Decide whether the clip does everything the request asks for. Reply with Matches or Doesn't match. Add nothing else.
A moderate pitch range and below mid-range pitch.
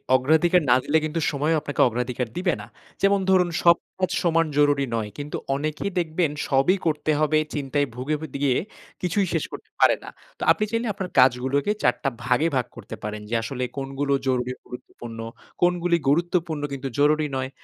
Doesn't match